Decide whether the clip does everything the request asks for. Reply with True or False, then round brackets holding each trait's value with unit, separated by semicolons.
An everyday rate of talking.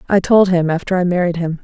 False (260 wpm)